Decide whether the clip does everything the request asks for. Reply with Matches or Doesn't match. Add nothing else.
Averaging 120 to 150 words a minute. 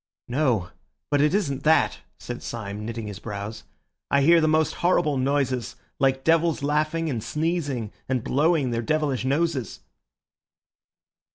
Matches